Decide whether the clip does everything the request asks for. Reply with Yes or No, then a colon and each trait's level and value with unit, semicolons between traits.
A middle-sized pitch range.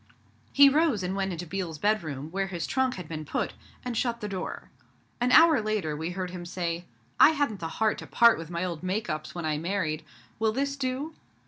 No: wide, 5.8 semitones